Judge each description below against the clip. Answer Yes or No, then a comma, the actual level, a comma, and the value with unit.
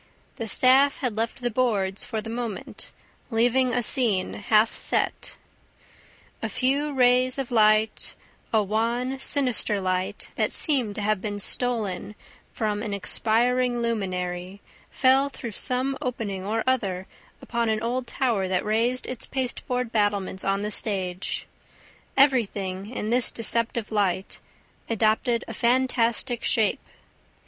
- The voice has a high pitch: Yes, high, 225 Hz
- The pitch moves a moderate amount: Yes, average, 3.5 semitones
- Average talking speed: No, slow, 130 wpm